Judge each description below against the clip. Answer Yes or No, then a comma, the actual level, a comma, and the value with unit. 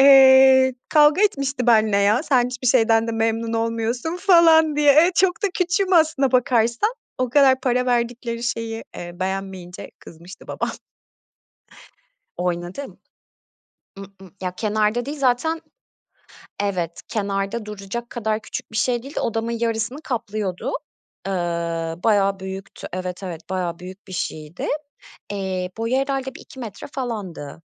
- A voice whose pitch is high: Yes, high, 230 Hz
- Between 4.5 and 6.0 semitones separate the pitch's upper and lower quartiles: Yes, average, 5.3 semitones